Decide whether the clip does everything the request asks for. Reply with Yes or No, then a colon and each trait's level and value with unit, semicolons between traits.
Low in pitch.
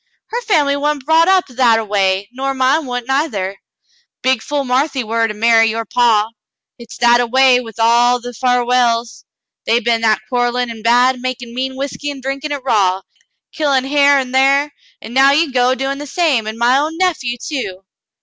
No: very high, 250 Hz